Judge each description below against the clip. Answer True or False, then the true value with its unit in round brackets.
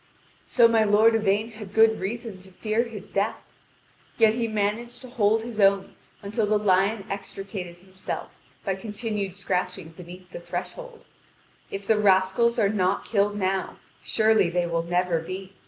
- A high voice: True (200 Hz)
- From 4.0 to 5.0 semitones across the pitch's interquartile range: False (2.8 semitones)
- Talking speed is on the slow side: False (155 wpm)